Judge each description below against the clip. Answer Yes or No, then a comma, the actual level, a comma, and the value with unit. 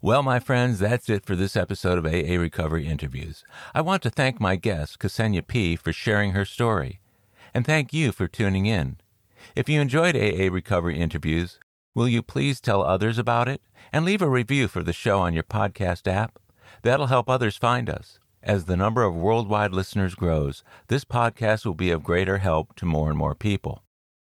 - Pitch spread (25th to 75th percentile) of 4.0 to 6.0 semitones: Yes, average, 5.1 semitones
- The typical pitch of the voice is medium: No, low, 105 Hz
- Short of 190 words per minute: No, average, 195 wpm